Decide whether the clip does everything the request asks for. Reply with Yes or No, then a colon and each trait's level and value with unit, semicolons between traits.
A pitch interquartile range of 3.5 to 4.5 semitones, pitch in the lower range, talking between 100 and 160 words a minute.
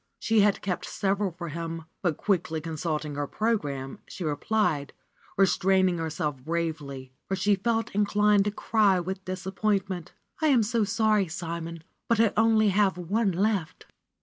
No: average, 4.2 semitones; high, 190 Hz; average, 150 wpm